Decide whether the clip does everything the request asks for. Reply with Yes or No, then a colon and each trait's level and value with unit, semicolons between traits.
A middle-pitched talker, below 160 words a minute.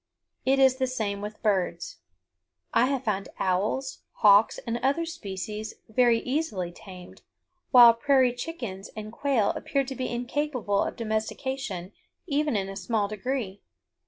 No: high, 230 Hz; average, 140 wpm